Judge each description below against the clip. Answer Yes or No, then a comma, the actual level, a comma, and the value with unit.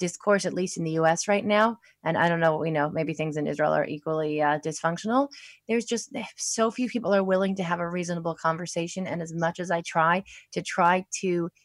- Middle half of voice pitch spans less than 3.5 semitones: No, average, 3.8 semitones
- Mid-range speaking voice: Yes, medium, 175 Hz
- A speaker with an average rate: No, fast, 230 wpm